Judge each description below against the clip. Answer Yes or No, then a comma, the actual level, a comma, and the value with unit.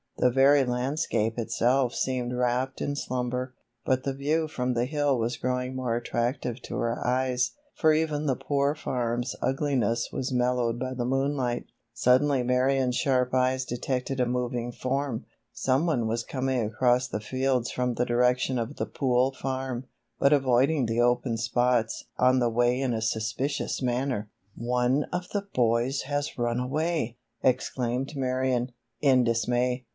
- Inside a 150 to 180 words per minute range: Yes, average, 155 wpm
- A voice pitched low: Yes, low, 125 Hz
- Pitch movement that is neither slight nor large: No, narrow, 1.7 semitones